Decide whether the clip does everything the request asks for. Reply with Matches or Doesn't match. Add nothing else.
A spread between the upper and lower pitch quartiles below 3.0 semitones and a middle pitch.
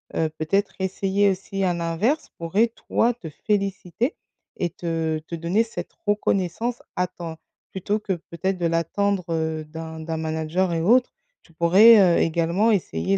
Doesn't match